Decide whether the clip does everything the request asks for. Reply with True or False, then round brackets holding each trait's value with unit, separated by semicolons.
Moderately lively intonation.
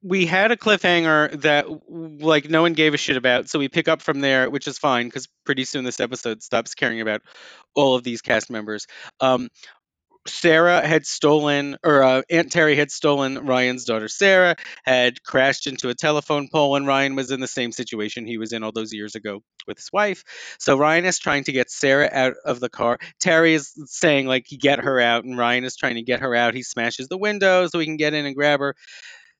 True (3.8 semitones)